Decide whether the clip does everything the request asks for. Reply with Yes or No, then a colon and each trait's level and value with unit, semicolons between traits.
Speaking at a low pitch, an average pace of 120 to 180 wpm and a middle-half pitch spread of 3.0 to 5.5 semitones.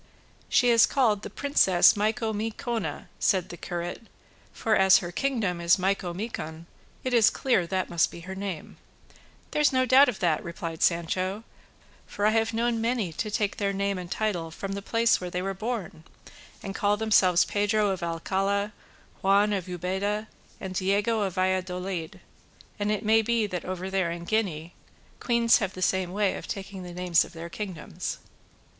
No: high, 195 Hz; average, 170 wpm; average, 3.4 semitones